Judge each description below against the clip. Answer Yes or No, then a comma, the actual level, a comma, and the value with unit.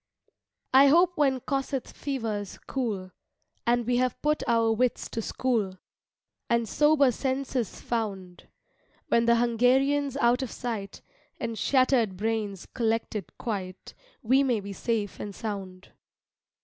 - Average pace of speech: No, slow, 125 wpm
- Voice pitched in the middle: No, high, 235 Hz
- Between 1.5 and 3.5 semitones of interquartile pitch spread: No, average, 3.9 semitones